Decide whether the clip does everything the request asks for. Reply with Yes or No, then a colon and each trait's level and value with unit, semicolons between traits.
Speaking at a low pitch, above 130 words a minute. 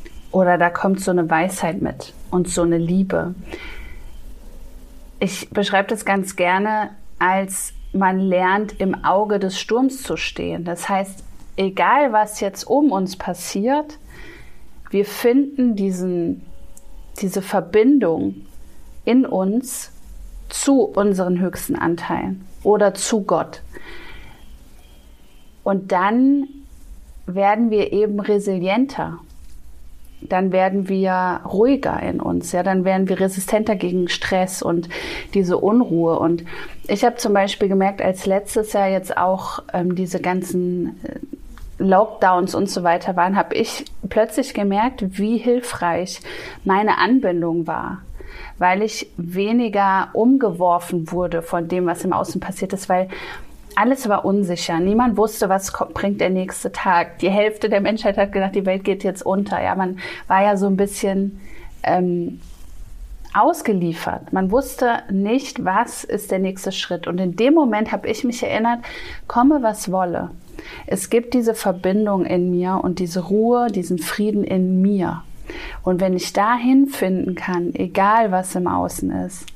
No: high, 195 Hz; average, 140 wpm